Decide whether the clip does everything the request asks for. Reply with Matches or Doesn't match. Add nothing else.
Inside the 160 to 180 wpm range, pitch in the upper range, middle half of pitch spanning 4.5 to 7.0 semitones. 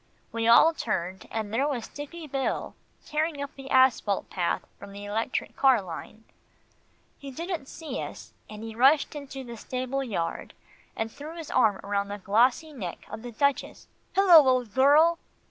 Matches